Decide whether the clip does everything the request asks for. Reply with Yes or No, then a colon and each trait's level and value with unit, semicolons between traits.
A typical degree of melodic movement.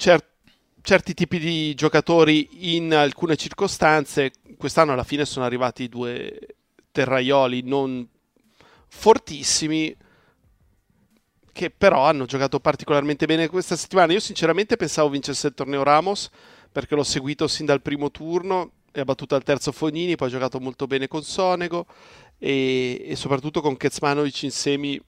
Yes: average, 3.2 semitones